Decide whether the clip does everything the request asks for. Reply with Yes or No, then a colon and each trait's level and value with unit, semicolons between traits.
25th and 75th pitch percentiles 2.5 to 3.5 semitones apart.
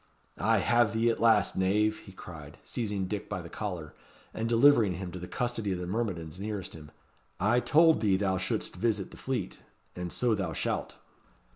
No: average, 4.0 semitones